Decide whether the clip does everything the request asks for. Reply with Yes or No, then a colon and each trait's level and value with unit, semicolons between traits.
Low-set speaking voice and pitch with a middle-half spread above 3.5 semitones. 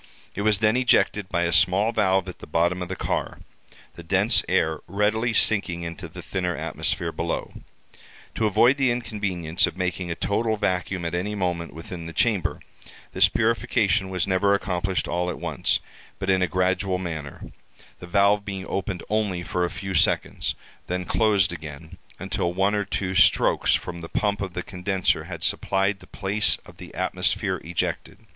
No: very low, 95 Hz; average, 2.7 semitones